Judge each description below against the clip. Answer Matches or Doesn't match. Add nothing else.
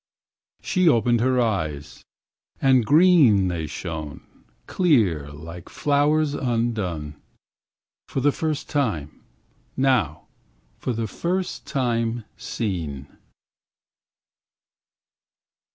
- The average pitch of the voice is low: Matches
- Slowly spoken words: Matches